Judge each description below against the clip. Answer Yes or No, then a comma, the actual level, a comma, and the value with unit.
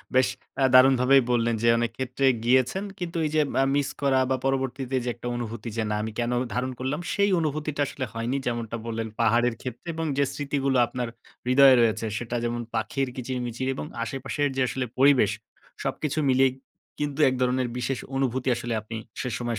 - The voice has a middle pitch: No, low, 130 Hz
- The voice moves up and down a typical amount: No, narrow, 2.3 semitones